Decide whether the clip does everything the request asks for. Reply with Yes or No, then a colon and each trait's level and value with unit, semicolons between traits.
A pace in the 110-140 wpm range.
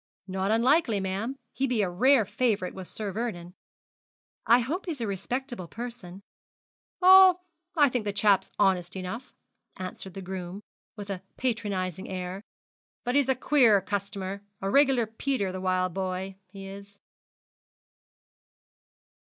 Yes: slow, 135 wpm